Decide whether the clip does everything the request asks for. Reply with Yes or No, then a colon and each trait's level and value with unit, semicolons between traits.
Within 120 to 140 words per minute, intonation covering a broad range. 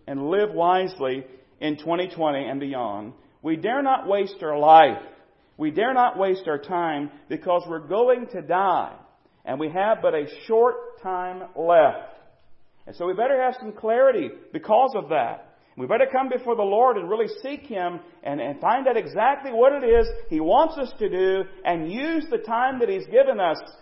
No: average, 185 wpm; wide, 8.2 semitones